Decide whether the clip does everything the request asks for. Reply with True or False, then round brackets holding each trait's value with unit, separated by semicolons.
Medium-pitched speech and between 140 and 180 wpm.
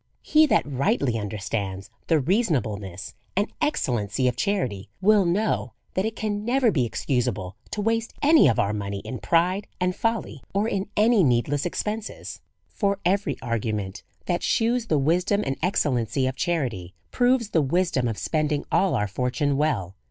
True (150 Hz; 160 wpm)